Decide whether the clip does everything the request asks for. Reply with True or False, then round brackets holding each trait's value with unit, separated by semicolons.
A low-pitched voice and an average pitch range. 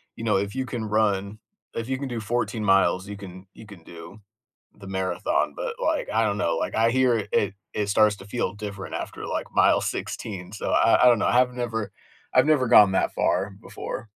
True (105 Hz; 3.6 semitones)